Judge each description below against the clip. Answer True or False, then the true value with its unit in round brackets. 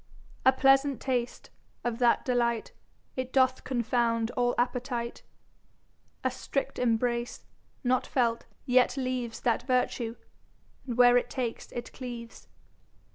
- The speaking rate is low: True (115 wpm)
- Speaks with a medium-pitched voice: False (245 Hz)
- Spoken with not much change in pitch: True (1.4 semitones)